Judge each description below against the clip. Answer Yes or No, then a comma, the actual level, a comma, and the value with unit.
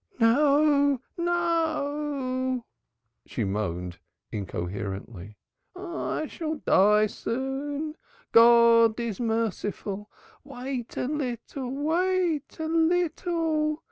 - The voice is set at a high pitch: Yes, very high, 270 Hz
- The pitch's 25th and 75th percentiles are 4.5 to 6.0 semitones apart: Yes, wide, 5.5 semitones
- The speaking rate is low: Yes, slow, 80 wpm